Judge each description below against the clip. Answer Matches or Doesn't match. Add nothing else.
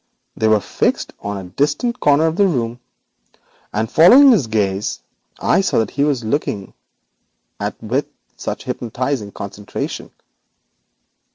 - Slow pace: Matches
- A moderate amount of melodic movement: Doesn't match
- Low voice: Matches